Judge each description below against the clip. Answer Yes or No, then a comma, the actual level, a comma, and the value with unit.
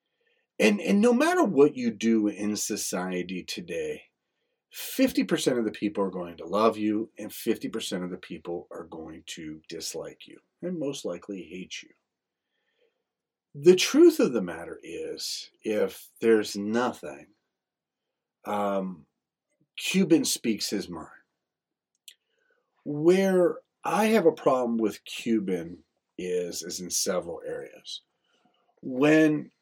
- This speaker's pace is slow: Yes, slow, 125 wpm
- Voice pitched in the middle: Yes, medium, 145 Hz